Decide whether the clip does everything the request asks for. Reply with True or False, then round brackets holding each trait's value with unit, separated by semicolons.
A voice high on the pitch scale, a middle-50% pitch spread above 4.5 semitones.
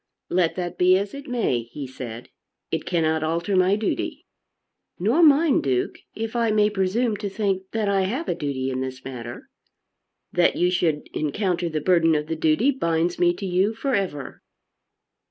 False (180 Hz; 5.1 semitones)